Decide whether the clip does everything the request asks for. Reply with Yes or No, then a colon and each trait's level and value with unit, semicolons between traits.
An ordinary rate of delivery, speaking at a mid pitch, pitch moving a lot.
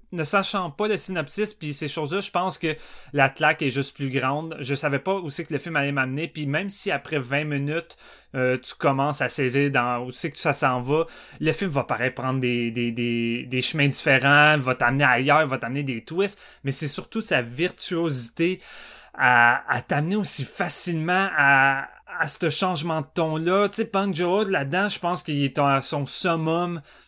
No: average, 205 wpm; medium, 150 Hz; average, 4.4 semitones